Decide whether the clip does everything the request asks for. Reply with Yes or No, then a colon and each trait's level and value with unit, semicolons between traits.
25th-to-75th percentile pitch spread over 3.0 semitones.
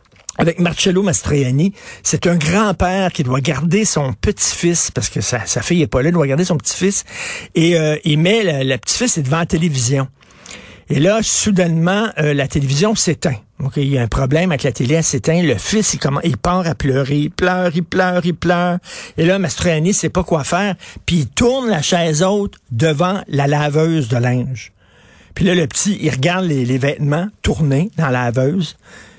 Yes: average, 4.6 semitones